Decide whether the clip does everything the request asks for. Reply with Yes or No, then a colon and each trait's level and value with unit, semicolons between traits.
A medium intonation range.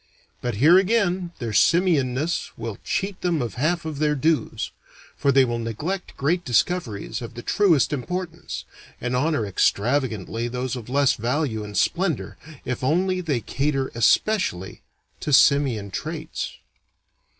No: wide, 6.1 semitones